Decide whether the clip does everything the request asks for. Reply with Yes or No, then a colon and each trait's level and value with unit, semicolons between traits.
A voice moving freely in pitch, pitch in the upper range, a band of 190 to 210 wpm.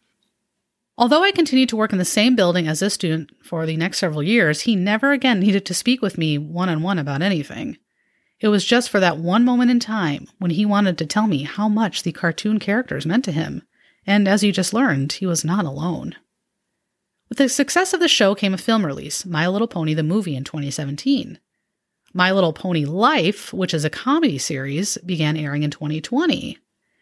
Yes: wide, 5.8 semitones; high, 195 Hz; fast, 205 wpm